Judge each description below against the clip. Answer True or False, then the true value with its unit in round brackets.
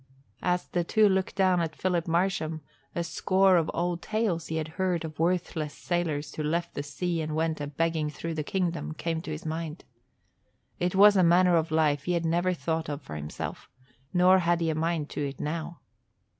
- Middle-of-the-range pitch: True (165 Hz)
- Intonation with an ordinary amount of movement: False (2.2 semitones)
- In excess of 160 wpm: True (200 wpm)